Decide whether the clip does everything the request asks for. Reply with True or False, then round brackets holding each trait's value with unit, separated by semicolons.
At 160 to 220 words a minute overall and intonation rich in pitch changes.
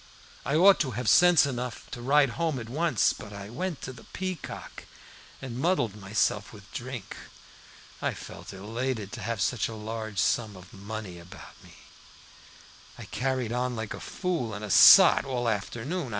False (175 wpm; 4.2 semitones)